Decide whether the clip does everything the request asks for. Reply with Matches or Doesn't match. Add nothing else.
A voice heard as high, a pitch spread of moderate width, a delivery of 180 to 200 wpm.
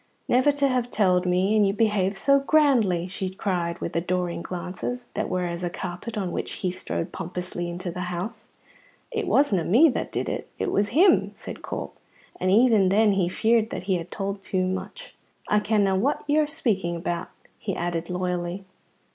Matches